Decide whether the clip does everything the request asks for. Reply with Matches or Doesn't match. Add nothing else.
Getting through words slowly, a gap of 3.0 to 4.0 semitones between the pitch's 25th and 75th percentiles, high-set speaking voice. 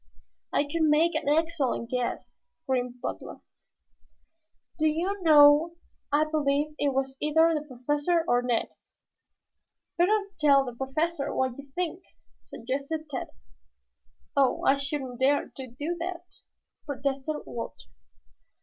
Matches